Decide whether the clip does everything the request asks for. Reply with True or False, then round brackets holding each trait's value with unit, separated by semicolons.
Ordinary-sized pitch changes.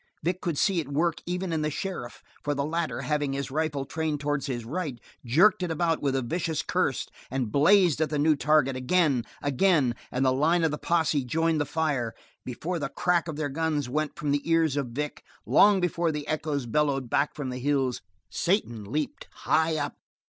True (3.2 semitones)